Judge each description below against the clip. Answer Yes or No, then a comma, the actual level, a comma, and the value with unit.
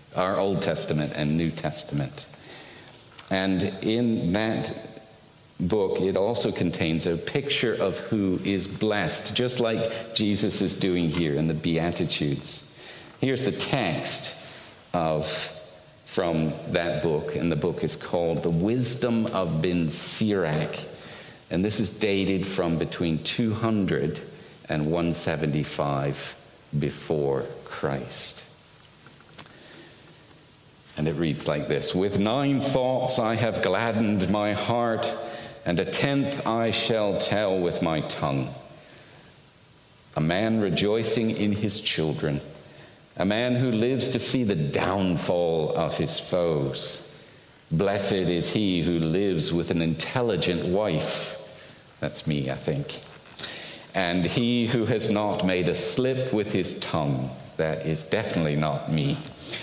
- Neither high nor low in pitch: No, very low, 95 Hz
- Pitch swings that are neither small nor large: No, wide, 6.0 semitones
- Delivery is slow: Yes, slow, 125 wpm